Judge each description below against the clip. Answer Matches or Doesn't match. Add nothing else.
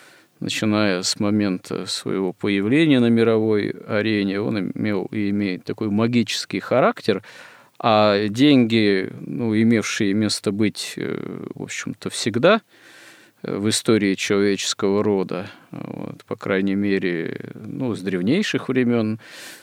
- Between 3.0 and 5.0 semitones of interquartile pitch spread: Doesn't match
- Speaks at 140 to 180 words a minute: Doesn't match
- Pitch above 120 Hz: Doesn't match